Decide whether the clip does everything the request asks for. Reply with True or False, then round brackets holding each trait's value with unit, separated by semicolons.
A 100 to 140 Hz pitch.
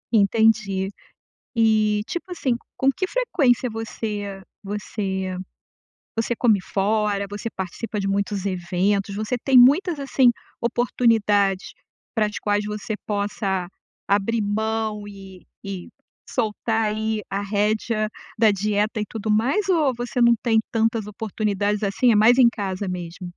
False (210 Hz)